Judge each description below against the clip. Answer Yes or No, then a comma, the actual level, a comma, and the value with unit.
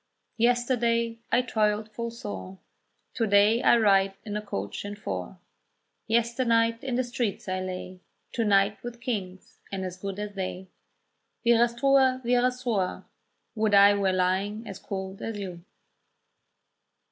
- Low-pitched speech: No, high, 210 Hz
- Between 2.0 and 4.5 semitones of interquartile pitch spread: Yes, average, 3.3 semitones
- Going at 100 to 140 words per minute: Yes, slow, 135 wpm